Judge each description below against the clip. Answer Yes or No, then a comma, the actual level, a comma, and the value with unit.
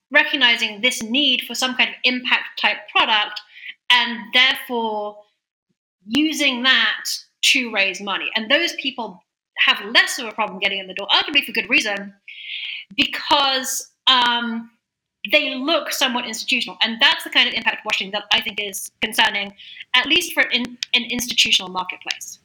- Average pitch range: Yes, average, 4.0 semitones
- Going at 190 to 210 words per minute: No, average, 160 wpm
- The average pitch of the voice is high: Yes, high, 245 Hz